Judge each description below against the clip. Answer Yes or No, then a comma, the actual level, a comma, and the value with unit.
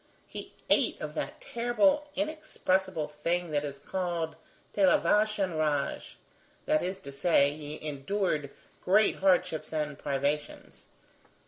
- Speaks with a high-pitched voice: No, medium, 170 Hz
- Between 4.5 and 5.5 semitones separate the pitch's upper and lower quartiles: Yes, average, 5.2 semitones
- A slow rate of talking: Yes, slow, 125 wpm